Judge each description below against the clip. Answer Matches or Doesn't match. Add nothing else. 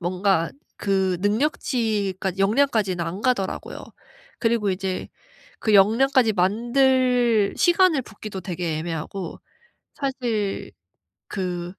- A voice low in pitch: Doesn't match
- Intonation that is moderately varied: Matches